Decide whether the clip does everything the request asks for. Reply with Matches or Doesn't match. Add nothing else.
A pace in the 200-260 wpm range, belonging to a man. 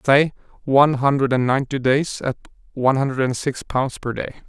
Doesn't match